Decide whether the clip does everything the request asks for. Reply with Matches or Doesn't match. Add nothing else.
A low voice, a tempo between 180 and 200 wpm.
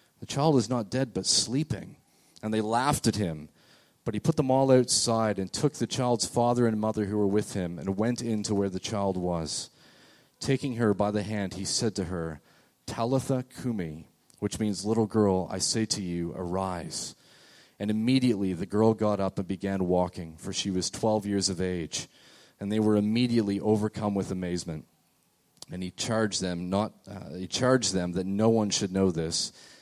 Matches